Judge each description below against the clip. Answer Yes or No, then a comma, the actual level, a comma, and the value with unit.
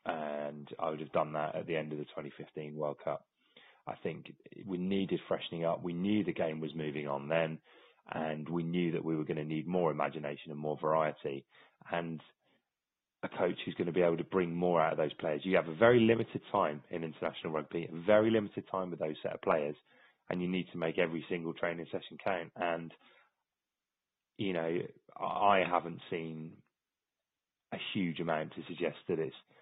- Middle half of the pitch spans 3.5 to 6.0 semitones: No, narrow, 2.6 semitones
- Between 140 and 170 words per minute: No, average, 195 wpm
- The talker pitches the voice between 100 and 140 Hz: No, very low, 80 Hz